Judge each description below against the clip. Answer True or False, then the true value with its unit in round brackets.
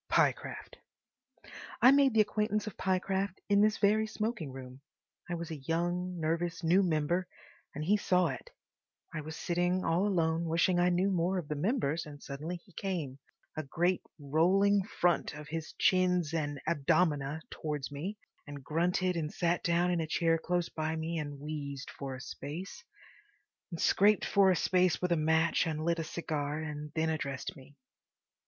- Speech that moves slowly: False (170 wpm)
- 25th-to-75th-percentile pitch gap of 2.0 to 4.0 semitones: True (3.2 semitones)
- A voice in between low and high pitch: True (170 Hz)